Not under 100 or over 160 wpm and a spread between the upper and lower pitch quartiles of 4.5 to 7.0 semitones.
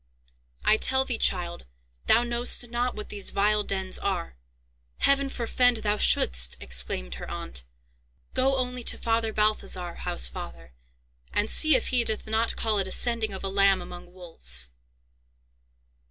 Yes: average, 150 wpm; average, 5.2 semitones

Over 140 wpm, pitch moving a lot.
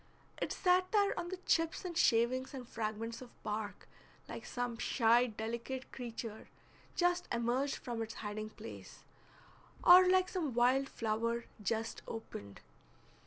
No: slow, 135 wpm; wide, 5.7 semitones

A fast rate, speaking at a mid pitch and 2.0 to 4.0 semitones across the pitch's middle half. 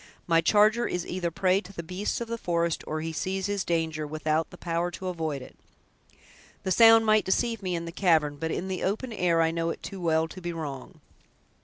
Yes: fast, 225 wpm; medium, 175 Hz; average, 2.9 semitones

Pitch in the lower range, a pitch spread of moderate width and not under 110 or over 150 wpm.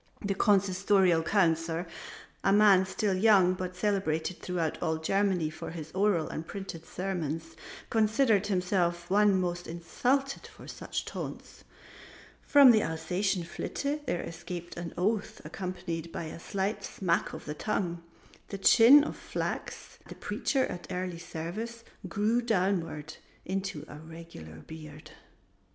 No: medium, 185 Hz; average, 3.5 semitones; slow, 135 wpm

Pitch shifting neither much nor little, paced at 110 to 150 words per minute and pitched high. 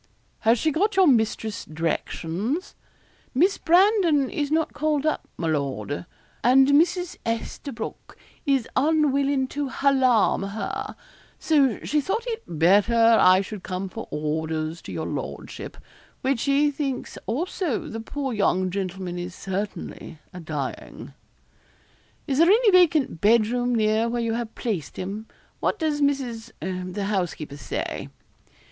No: wide, 7.6 semitones; slow, 135 wpm; high, 235 Hz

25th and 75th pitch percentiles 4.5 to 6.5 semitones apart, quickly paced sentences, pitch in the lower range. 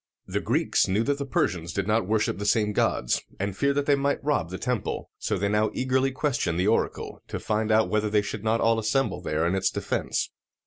Yes: average, 4.8 semitones; fast, 225 wpm; low, 110 Hz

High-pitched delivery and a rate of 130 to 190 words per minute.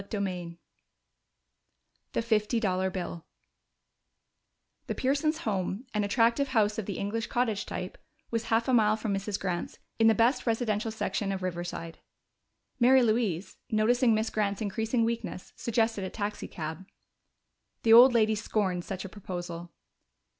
Yes: high, 215 Hz; average, 140 wpm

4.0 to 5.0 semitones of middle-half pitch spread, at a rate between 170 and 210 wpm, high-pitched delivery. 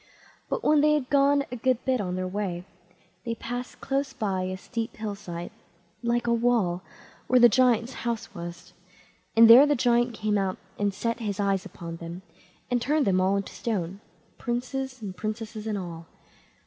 Yes: average, 4.4 semitones; average, 180 wpm; high, 225 Hz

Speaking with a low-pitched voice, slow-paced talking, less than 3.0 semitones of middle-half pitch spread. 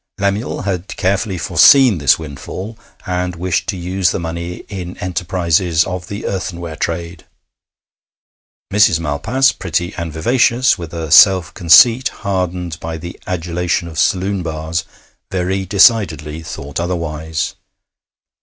Yes: very low, 90 Hz; slow, 125 wpm; narrow, 2.6 semitones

